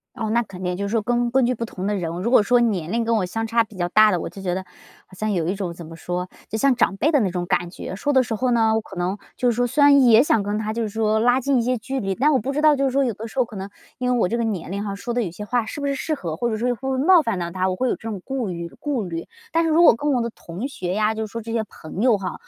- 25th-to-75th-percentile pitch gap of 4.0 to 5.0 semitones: Yes, average, 4.5 semitones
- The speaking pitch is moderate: No, high, 220 Hz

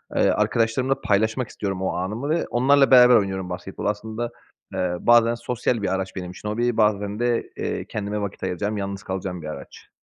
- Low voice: Yes, low, 105 Hz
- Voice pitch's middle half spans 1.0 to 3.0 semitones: No, average, 3.7 semitones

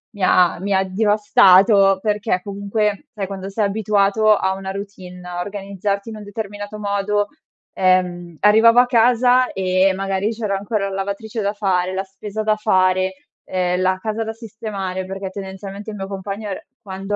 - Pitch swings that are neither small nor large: No, narrow, 1.9 semitones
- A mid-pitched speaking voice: No, high, 200 Hz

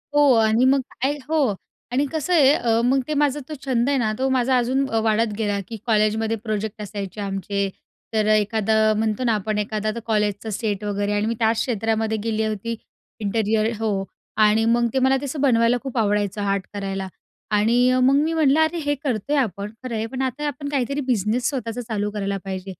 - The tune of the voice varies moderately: Yes, average, 3.7 semitones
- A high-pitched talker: Yes, high, 225 Hz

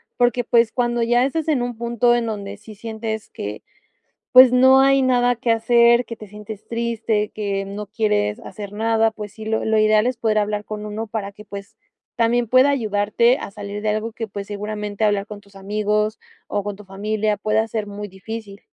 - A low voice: No, high, 215 Hz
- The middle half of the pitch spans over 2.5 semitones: No, narrow, 2.2 semitones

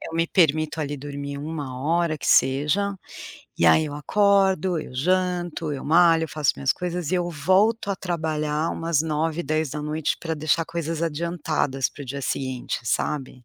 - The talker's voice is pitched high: No, medium, 155 Hz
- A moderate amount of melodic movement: Yes, average, 3.0 semitones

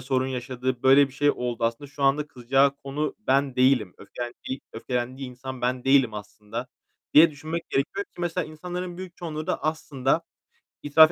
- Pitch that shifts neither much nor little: Yes, average, 3.4 semitones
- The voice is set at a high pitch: No, low, 135 Hz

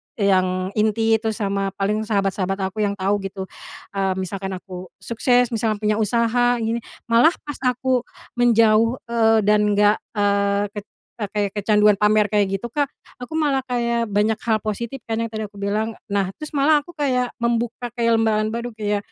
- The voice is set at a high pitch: Yes, high, 215 Hz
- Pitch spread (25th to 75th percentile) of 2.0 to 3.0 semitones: Yes, narrow, 2.6 semitones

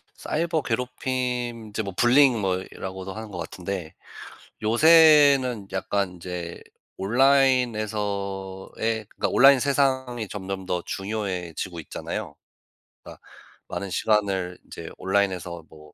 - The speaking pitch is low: Yes, low, 105 Hz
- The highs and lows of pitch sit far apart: No, average, 4.9 semitones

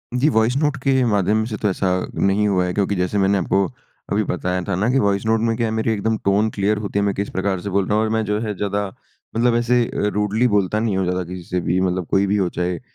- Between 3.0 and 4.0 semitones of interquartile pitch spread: No, narrow, 2.5 semitones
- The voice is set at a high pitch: No, low, 100 Hz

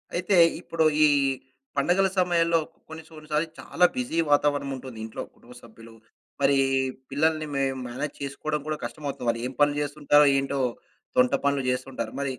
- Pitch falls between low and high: Yes, medium, 145 Hz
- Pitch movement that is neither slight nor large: Yes, average, 3.2 semitones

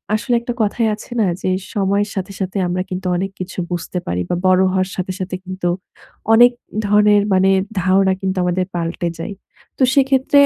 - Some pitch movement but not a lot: No, narrow, 2.1 semitones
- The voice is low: No, high, 190 Hz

